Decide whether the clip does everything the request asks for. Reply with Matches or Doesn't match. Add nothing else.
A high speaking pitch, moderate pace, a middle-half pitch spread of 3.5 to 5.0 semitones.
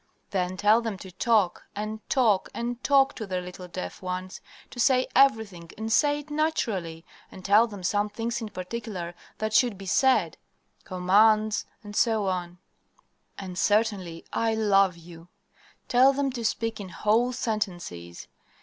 Matches